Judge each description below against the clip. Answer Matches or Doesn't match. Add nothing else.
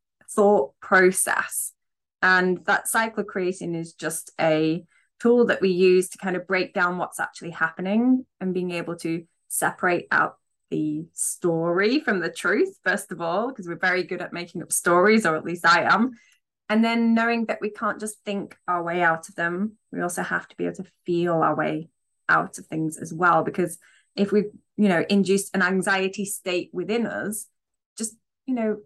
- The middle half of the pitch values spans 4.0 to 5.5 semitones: Doesn't match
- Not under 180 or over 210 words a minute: Matches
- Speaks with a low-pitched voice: Doesn't match